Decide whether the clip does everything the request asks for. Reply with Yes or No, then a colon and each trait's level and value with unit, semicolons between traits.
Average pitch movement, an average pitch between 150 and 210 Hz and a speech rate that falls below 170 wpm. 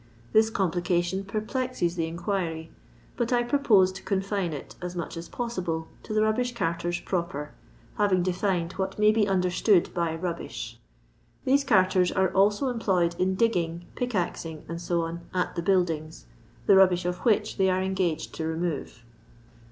Yes: average, 3.4 semitones; medium, 185 Hz; average, 155 wpm